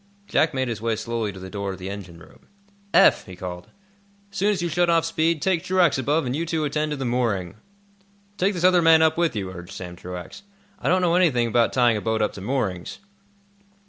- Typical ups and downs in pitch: No, wide, 8.7 semitones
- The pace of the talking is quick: Yes, fast, 230 wpm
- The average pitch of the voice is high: No, low, 125 Hz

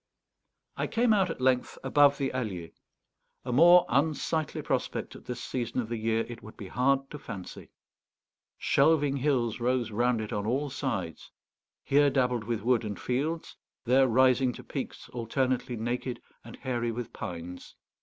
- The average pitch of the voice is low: Yes, low, 125 Hz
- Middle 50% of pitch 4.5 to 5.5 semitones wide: No, average, 3.2 semitones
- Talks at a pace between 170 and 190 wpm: No, average, 160 wpm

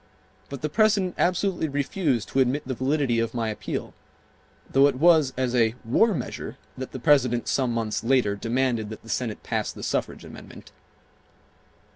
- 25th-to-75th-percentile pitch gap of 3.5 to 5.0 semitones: Yes, average, 4.1 semitones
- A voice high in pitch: No, low, 130 Hz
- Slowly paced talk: No, average, 165 wpm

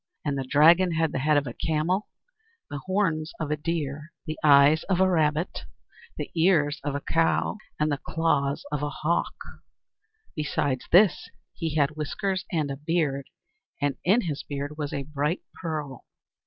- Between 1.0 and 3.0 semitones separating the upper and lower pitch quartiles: Yes, narrow, 2.6 semitones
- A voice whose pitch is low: No, medium, 155 Hz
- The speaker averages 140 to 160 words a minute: No, average, 170 wpm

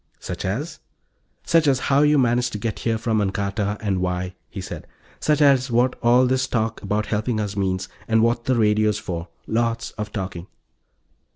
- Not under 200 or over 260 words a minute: No, average, 180 wpm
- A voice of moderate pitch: No, low, 110 Hz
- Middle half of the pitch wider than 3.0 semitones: Yes, average, 3.7 semitones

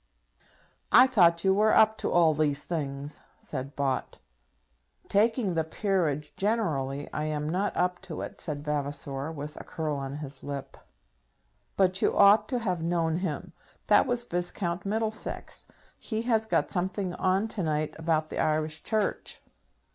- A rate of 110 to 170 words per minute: Yes, average, 155 wpm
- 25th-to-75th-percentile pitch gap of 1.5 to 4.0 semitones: No, average, 5.2 semitones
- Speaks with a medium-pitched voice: Yes, medium, 170 Hz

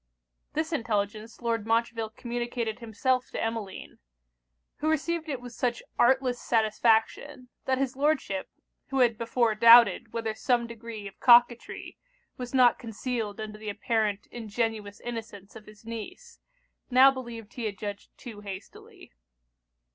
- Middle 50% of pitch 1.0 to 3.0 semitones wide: Yes, narrow, 2.4 semitones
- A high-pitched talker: Yes, high, 230 Hz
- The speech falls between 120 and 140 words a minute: Yes, slow, 135 wpm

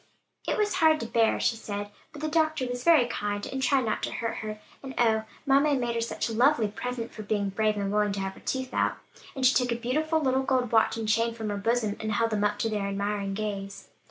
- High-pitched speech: Yes, high, 230 Hz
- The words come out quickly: Yes, fast, 255 wpm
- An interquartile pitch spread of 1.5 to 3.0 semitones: No, average, 3.9 semitones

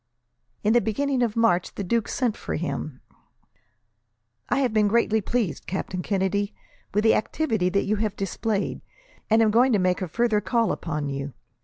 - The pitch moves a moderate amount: Yes, average, 3.8 semitones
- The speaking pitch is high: Yes, high, 210 Hz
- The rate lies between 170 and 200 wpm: Yes, average, 175 wpm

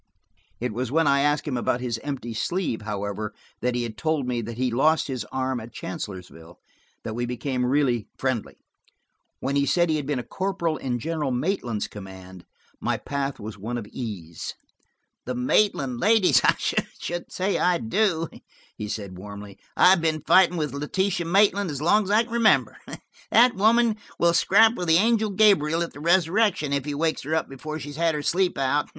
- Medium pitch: Yes, medium, 145 Hz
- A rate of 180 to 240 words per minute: Yes, average, 190 wpm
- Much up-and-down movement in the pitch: Yes, wide, 6.4 semitones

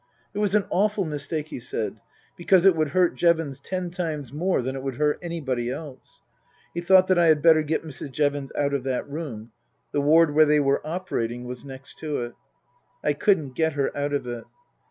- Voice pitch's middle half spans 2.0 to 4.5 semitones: Yes, average, 3.9 semitones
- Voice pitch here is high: No, medium, 150 Hz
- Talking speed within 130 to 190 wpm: No, fast, 205 wpm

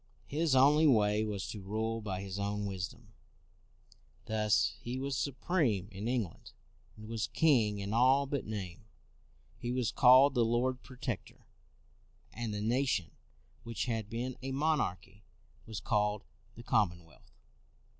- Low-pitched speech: Yes, low, 115 Hz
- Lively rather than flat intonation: No, average, 3.9 semitones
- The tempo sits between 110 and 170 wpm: Yes, average, 140 wpm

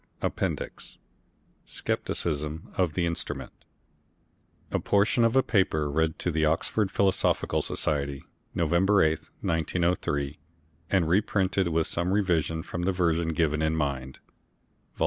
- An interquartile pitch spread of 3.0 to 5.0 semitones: Yes, average, 3.3 semitones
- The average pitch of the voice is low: Yes, very low, 85 Hz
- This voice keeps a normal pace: No, slow, 125 wpm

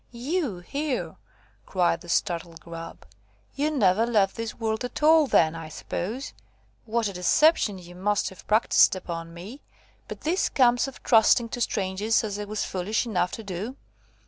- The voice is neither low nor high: No, high, 210 Hz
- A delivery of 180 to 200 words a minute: No, average, 165 wpm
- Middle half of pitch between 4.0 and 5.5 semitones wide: Yes, average, 5.2 semitones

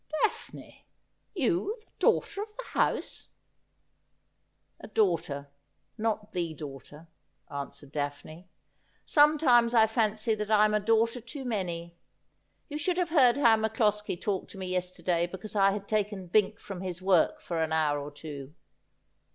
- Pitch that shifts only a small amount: No, average, 5.1 semitones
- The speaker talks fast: No, average, 160 wpm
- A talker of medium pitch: No, high, 205 Hz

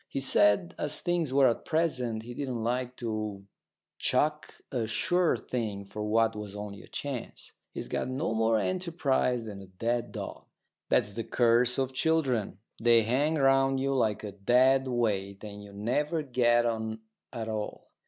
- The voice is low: Yes, low, 120 Hz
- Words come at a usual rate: Yes, average, 165 wpm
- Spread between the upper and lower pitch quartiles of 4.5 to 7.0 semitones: No, average, 3.8 semitones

